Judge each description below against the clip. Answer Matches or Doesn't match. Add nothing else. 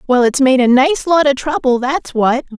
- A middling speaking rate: Doesn't match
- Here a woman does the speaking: Matches